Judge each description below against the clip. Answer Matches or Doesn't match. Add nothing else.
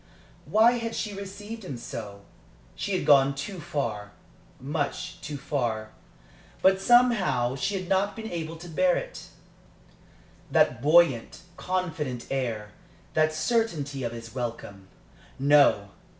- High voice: Doesn't match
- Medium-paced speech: Doesn't match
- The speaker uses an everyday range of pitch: Doesn't match